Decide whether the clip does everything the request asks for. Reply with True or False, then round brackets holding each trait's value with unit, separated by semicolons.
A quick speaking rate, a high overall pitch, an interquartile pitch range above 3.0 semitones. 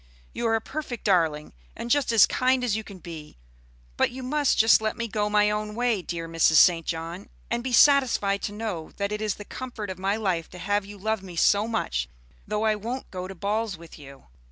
True (225 wpm; 210 Hz; 4.0 semitones)